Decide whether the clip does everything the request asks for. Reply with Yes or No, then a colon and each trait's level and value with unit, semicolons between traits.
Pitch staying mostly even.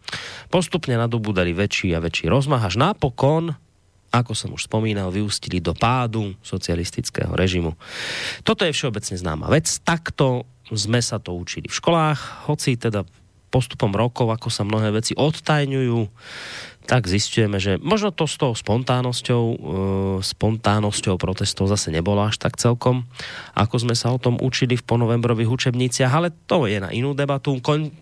No: average, 4.5 semitones